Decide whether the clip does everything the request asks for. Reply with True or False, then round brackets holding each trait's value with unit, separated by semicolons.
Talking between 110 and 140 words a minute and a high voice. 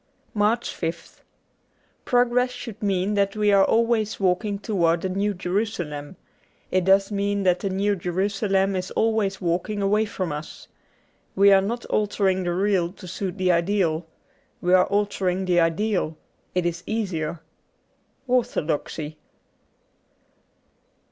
True (135 wpm; 195 Hz)